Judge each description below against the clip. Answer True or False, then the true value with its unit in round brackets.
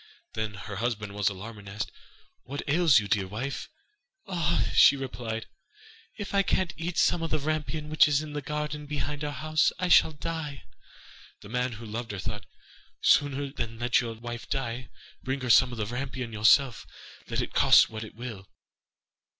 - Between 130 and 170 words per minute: False (185 wpm)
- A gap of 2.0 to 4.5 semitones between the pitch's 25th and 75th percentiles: False (5.1 semitones)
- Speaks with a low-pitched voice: True (130 Hz)